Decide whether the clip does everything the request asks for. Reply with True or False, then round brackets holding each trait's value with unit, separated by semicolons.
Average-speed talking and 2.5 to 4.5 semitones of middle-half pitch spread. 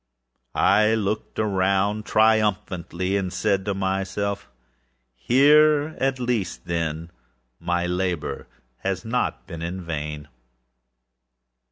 False (95 wpm; 3.6 semitones)